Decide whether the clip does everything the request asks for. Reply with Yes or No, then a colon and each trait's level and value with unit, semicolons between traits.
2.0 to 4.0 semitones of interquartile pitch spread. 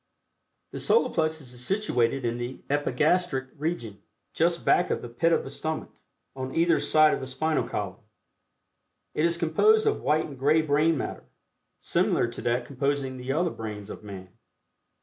No: average, 4.8 semitones